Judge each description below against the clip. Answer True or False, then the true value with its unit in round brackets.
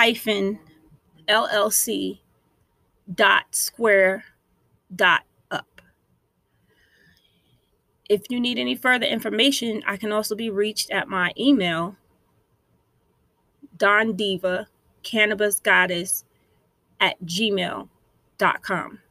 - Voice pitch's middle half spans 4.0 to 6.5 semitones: False (2.9 semitones)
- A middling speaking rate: False (80 wpm)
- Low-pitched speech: False (210 Hz)